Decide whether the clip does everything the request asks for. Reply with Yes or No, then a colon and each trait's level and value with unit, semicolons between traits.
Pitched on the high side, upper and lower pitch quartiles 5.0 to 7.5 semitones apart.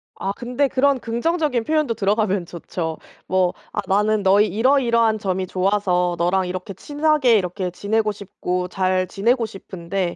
No: high, 205 Hz; average, 4.0 semitones